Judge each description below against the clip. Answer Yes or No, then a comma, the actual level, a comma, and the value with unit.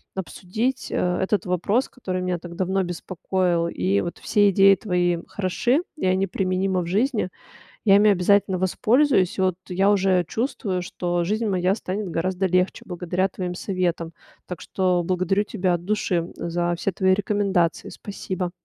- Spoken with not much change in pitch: Yes, narrow, 2.0 semitones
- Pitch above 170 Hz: Yes, medium, 185 Hz